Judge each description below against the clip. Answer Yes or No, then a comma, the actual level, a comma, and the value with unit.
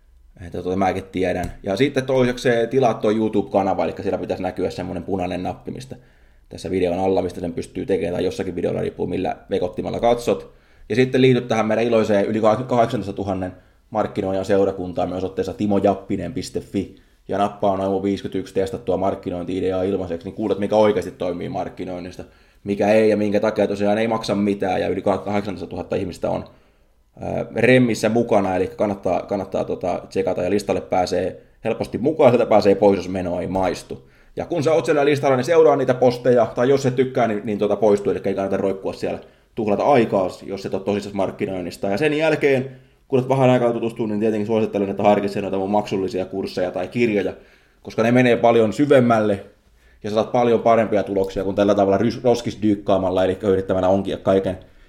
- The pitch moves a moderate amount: Yes, average, 3.3 semitones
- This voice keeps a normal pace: No, fast, 175 wpm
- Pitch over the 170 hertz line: No, low, 100 Hz